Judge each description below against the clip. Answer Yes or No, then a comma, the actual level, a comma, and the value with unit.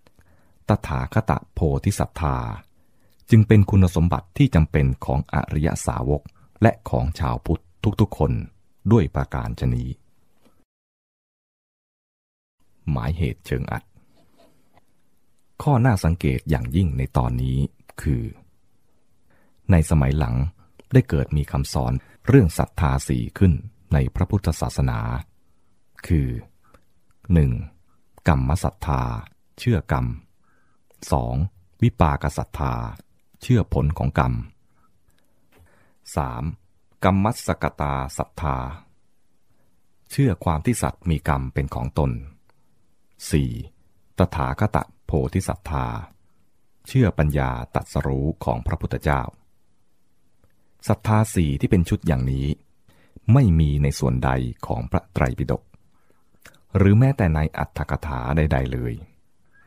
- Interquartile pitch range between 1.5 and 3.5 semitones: No, wide, 5.5 semitones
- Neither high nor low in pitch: No, very low, 80 Hz